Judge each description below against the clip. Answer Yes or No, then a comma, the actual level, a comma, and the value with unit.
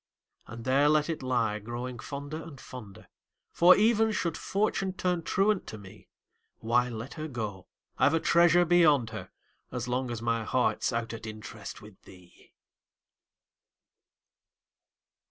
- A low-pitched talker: Yes, low, 130 Hz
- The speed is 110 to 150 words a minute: Yes, average, 140 wpm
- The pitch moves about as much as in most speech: No, wide, 6.7 semitones